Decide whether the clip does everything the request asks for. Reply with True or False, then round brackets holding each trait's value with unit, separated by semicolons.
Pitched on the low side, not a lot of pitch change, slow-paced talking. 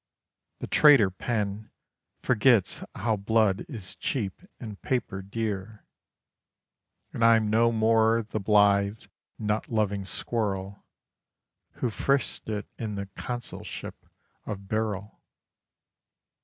True (110 Hz; 2.3 semitones; 100 wpm)